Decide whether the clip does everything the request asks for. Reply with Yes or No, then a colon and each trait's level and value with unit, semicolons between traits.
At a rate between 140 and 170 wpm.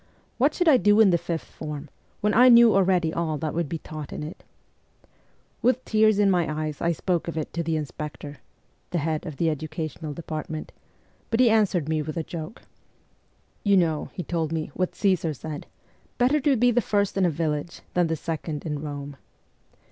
No: average, 195 wpm